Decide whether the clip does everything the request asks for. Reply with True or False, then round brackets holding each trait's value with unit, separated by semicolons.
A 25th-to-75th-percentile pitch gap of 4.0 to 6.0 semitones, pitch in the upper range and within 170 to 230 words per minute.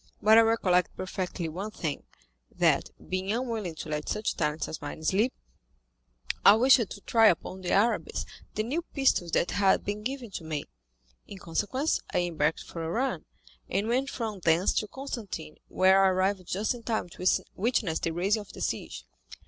True (4.5 semitones; 195 Hz; 175 wpm)